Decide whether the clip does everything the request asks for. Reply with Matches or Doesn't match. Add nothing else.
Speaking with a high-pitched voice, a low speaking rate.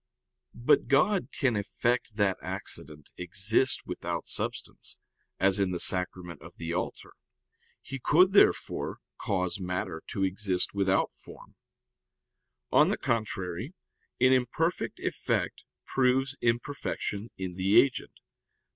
Doesn't match